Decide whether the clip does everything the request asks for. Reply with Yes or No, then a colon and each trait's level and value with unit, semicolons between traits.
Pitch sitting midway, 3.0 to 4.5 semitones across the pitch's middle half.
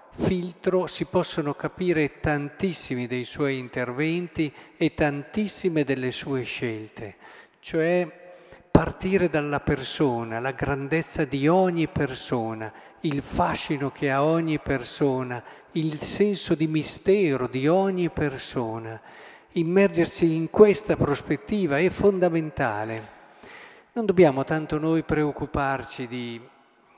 Yes: medium, 150 Hz; average, 4.1 semitones